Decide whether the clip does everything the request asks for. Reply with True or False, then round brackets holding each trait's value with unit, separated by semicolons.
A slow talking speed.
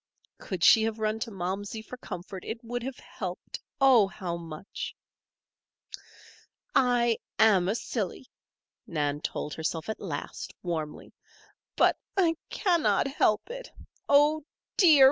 True (125 wpm)